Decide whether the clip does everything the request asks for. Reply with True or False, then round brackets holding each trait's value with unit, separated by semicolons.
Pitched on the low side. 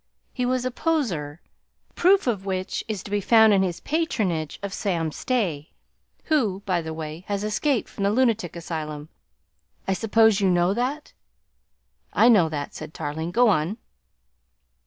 False (200 Hz)